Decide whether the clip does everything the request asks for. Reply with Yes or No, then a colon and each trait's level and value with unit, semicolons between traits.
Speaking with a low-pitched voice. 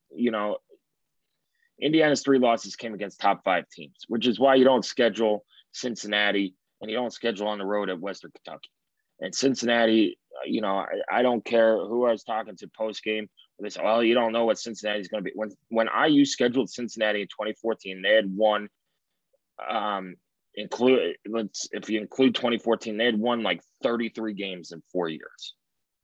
Yes: low, 115 Hz